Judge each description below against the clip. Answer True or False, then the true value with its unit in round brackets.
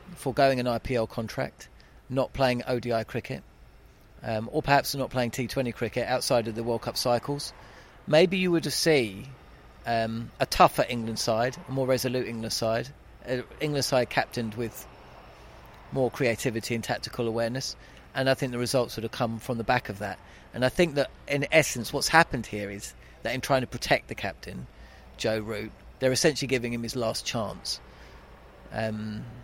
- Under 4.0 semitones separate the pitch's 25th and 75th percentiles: True (2.8 semitones)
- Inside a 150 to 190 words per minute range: True (175 wpm)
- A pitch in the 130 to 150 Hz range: False (120 Hz)